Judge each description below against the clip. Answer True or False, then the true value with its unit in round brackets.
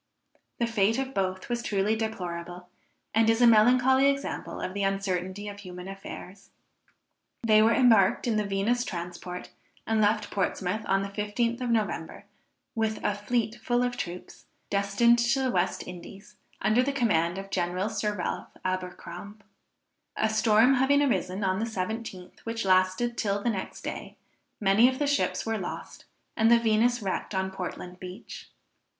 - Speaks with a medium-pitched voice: False (210 Hz)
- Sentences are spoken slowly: False (160 wpm)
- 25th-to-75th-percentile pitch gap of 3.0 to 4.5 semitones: True (3.7 semitones)